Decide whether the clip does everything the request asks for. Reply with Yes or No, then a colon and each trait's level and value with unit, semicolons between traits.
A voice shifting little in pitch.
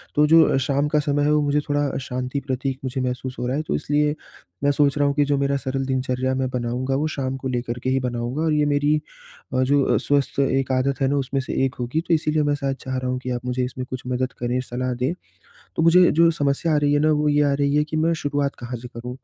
Yes: narrow, 2.3 semitones